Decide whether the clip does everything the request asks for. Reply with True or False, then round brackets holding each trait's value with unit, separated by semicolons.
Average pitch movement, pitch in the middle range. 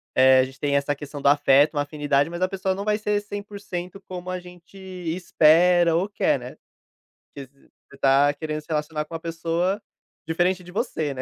True (4.1 semitones; 165 Hz)